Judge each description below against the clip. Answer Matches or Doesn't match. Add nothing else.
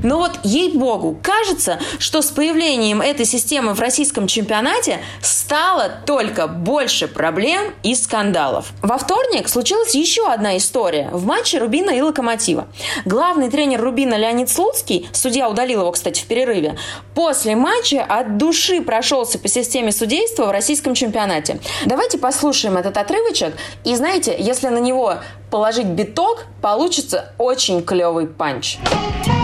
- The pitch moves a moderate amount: Doesn't match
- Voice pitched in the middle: Doesn't match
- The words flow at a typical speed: Matches